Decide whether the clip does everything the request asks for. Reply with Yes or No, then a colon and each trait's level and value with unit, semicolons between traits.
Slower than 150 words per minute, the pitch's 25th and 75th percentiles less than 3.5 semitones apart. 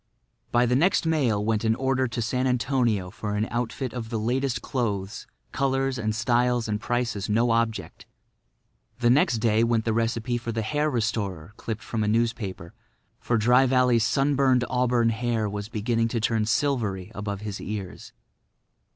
No: average, 165 wpm; narrow, 2.6 semitones